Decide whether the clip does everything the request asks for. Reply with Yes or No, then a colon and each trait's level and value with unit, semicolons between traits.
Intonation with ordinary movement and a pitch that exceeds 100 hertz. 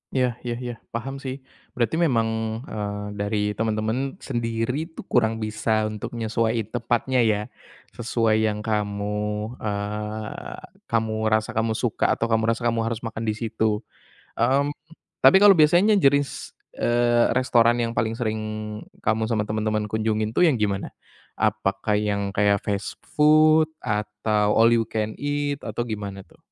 No: narrow, 2.1 semitones; low, 110 Hz